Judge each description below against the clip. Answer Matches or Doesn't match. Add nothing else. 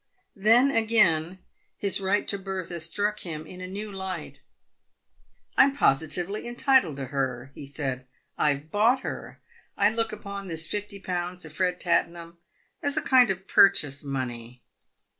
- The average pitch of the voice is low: Doesn't match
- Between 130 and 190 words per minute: Matches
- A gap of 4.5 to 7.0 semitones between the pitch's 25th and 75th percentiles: Matches